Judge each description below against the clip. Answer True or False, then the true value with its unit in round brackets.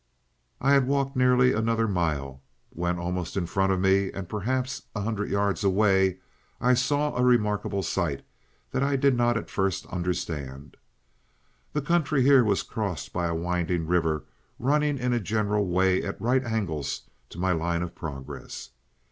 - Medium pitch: False (100 Hz)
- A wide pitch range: True (6.1 semitones)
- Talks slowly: False (165 wpm)